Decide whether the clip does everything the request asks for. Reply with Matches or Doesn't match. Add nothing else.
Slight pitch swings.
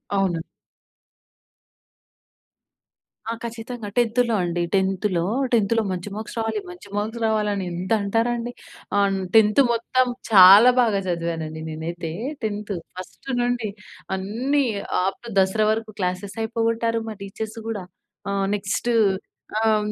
Doesn't match